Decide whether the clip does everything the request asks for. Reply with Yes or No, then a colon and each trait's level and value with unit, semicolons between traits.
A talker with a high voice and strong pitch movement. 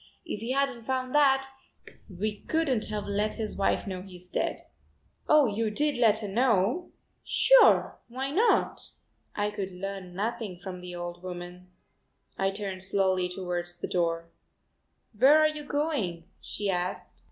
Yes: high, 205 Hz; wide, 6.1 semitones